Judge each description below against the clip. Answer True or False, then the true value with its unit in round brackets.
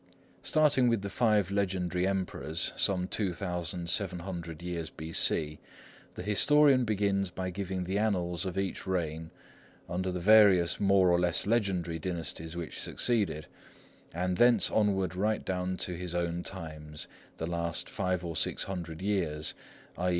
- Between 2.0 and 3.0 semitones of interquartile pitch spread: True (2.6 semitones)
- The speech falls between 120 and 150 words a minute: True (140 wpm)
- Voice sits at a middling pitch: False (90 Hz)